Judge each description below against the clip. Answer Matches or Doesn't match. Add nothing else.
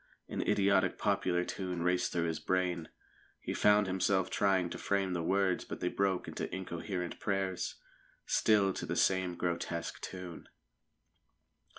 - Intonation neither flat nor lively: Doesn't match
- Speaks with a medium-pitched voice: Doesn't match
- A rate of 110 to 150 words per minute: Matches